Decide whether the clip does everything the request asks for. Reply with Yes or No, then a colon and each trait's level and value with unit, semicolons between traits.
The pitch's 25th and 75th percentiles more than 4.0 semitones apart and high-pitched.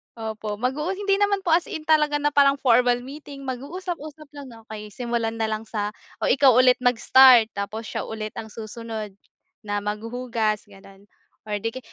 Yes: average, 4.8 semitones; high, 245 Hz